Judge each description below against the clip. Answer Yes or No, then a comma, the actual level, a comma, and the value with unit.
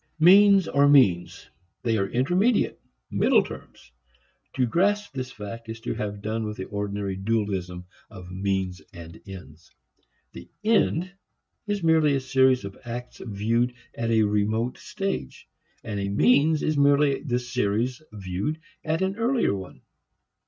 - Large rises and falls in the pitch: Yes, wide, 6.8 semitones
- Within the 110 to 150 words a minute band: Yes, average, 145 wpm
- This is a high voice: No, low, 115 Hz